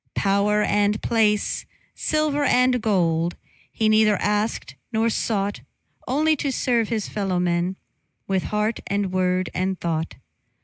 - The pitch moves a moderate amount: Yes, average, 3.3 semitones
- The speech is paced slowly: Yes, slow, 125 wpm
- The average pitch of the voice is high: Yes, high, 210 Hz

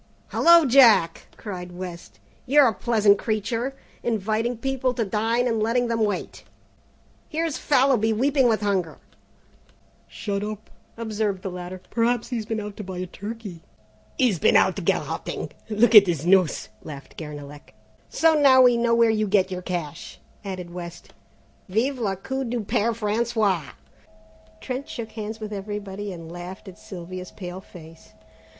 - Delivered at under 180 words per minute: Yes, average, 155 wpm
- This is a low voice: No, high, 215 Hz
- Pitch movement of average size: Yes, average, 4.2 semitones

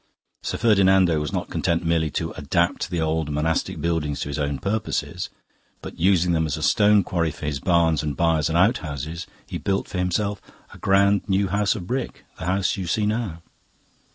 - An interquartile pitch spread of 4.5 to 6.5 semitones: No, average, 3.8 semitones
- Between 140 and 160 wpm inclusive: No, average, 190 wpm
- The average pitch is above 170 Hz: No, very low, 85 Hz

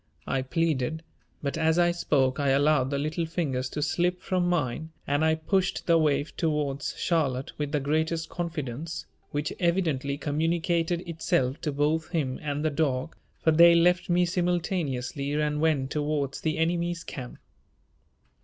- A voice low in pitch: No, medium, 155 Hz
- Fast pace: No, average, 155 wpm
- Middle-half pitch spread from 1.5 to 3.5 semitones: Yes, average, 3.1 semitones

